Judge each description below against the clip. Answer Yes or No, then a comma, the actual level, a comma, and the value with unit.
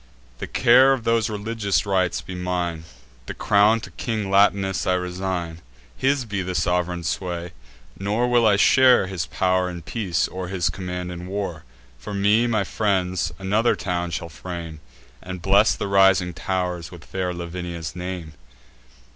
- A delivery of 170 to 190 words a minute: No, average, 155 wpm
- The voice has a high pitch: No, very low, 95 Hz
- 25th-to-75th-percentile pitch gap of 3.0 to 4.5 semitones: No, narrow, 2.5 semitones